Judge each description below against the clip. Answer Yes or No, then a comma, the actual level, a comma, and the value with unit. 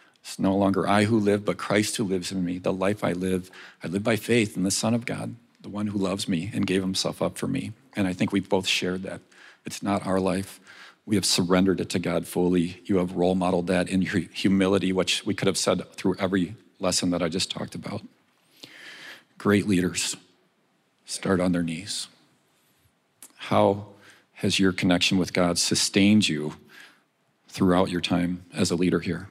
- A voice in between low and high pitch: No, very low, 95 Hz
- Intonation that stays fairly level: Yes, narrow, 2.0 semitones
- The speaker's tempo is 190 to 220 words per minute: Yes, average, 195 wpm